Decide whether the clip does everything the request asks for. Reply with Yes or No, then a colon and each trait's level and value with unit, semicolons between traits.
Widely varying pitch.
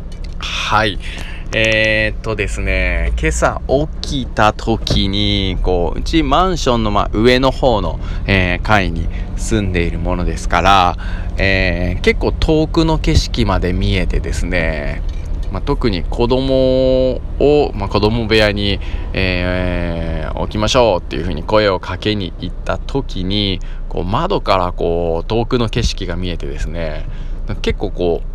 No: average, 4.4 semitones